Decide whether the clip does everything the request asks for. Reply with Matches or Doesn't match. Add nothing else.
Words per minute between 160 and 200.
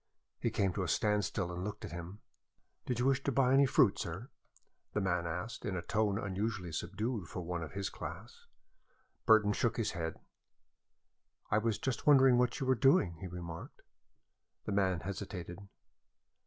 Matches